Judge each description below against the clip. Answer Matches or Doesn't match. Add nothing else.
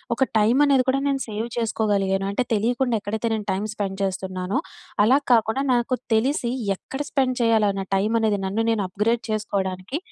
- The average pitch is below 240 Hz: Matches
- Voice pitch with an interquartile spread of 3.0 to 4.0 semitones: Matches